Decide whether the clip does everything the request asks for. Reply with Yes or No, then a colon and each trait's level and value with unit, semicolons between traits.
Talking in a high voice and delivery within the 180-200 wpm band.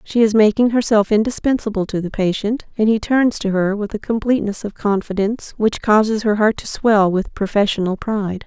Yes: high, 210 Hz; average, 190 wpm